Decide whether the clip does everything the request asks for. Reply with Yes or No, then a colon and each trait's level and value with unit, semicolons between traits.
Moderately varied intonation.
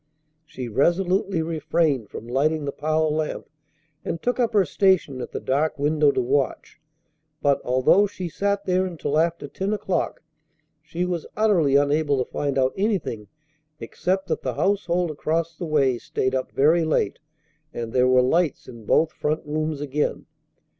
Yes: average, 4.2 semitones